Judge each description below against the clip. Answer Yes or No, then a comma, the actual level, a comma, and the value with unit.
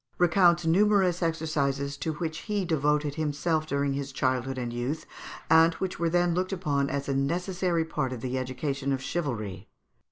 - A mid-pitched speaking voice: Yes, medium, 150 Hz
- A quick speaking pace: No, average, 165 wpm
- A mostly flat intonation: No, average, 3.9 semitones